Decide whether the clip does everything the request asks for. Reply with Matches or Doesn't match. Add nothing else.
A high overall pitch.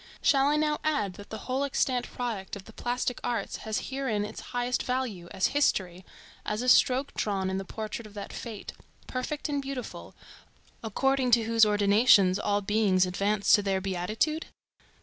Matches